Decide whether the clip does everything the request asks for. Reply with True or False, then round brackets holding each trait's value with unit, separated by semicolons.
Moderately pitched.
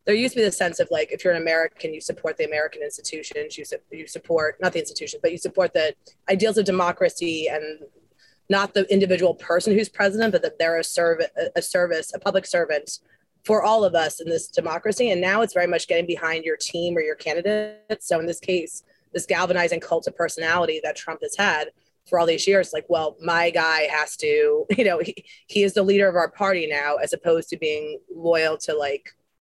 True (180 Hz)